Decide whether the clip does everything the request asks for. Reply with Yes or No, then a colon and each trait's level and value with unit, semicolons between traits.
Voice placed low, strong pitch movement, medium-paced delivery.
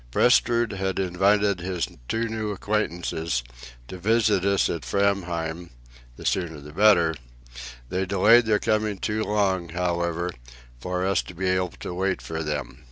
No: very low, 95 Hz; average, 3.3 semitones; average, 150 wpm